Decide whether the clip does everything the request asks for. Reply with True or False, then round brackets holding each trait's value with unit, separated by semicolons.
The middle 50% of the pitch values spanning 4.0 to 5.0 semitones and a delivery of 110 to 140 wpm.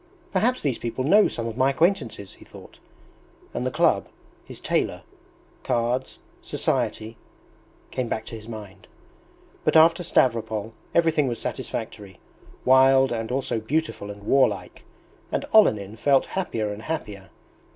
True (4.6 semitones; 135 wpm)